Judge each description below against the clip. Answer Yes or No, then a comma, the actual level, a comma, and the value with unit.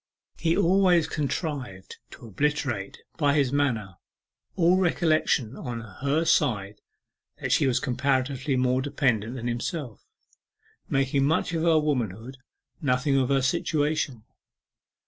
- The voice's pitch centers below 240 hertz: Yes, low, 135 Hz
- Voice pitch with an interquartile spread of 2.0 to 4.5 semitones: Yes, average, 3.9 semitones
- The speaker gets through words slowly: Yes, slow, 120 wpm